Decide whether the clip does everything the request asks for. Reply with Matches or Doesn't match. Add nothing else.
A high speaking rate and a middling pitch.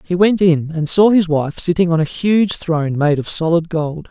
Matches